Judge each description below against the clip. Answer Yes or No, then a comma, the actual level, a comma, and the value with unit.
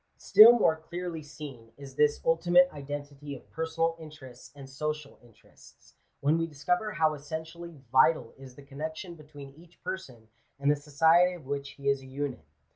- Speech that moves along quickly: No, average, 165 wpm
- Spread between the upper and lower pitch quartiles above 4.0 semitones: No, average, 2.9 semitones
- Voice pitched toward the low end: No, medium, 150 Hz